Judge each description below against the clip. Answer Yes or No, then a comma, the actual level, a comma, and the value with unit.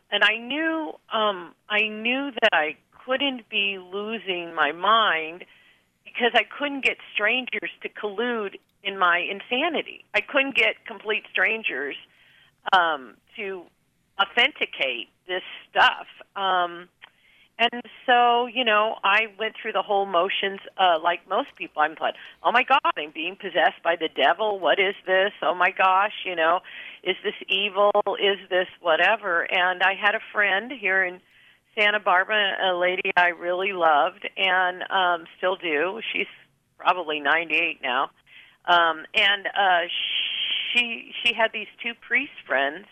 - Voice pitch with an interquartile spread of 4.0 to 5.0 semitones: No, average, 3.5 semitones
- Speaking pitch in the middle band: No, high, 195 Hz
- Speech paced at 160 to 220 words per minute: No, average, 150 wpm